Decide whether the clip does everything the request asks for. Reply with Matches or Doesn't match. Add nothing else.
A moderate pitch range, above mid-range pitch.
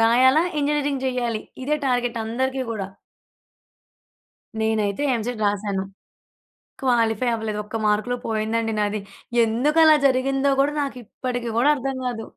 Matches